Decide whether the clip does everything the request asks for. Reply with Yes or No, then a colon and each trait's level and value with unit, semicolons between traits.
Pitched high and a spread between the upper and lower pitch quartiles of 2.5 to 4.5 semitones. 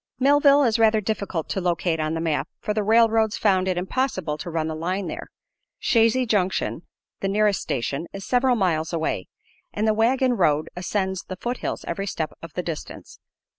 No: high, 195 Hz; average, 5.1 semitones